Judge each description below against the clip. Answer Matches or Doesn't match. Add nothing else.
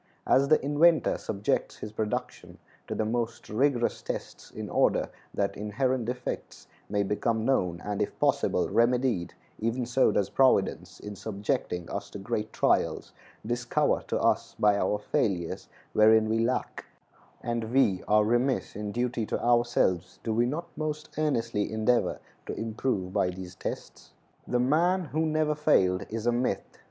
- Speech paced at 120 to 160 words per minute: Matches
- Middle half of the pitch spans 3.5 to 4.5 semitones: Matches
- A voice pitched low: Matches